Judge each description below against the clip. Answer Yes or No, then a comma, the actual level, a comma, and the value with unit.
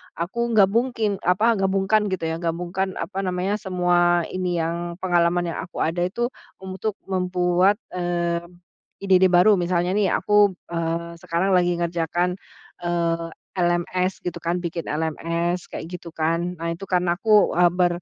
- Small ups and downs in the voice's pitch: Yes, narrow, 1.9 semitones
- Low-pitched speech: No, medium, 180 Hz